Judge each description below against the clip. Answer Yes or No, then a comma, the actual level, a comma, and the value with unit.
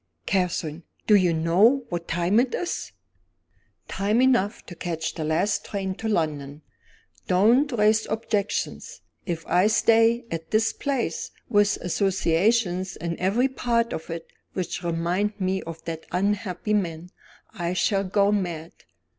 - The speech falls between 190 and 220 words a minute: No, average, 140 wpm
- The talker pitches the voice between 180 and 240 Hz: Yes, high, 190 Hz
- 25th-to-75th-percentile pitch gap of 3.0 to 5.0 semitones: Yes, average, 4.3 semitones